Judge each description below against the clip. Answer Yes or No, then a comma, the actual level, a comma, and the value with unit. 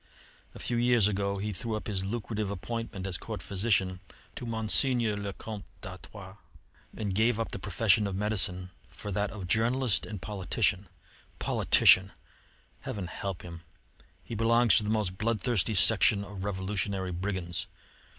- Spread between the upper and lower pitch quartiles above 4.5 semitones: No, average, 2.8 semitones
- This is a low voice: Yes, low, 105 Hz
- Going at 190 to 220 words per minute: No, average, 150 wpm